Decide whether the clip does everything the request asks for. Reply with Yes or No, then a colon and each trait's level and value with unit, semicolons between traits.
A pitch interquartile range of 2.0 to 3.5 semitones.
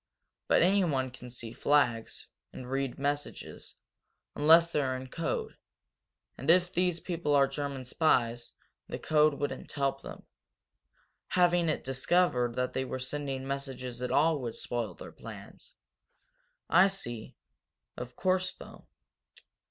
No: average, 4.6 semitones